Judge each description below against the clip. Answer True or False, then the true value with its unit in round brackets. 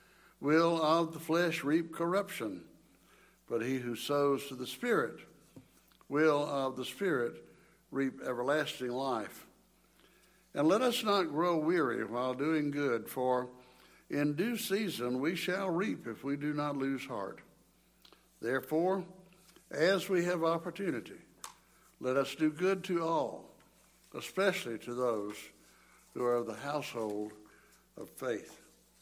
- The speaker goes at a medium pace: False (130 wpm)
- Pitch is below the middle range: False (145 Hz)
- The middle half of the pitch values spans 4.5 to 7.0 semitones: True (5.4 semitones)